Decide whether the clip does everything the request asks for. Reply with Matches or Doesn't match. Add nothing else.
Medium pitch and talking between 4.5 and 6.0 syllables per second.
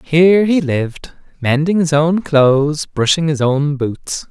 Doesn't match